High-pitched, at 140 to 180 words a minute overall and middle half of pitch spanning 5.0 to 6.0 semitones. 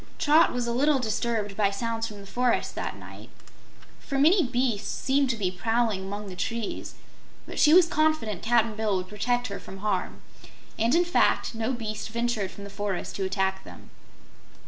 No: high, 225 Hz; average, 175 wpm; average, 3.7 semitones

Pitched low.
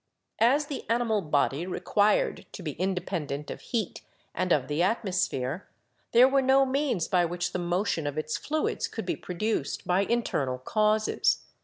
No: medium, 185 Hz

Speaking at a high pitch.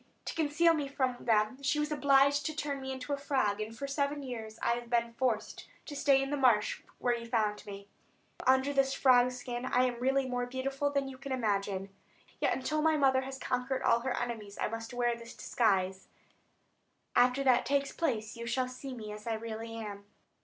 Yes: very high, 255 Hz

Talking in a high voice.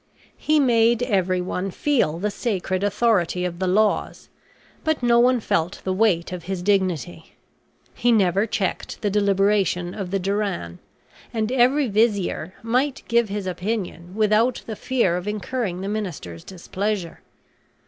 Yes: high, 200 Hz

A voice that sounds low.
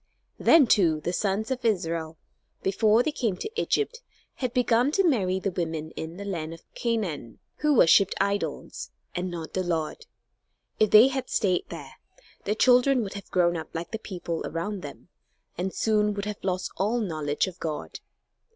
No: high, 195 Hz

